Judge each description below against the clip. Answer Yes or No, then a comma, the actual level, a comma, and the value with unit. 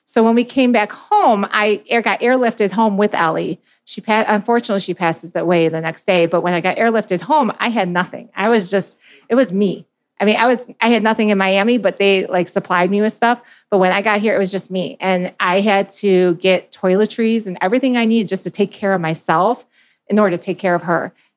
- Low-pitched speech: No, high, 200 Hz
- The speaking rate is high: Yes, fast, 235 wpm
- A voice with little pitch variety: No, average, 3.7 semitones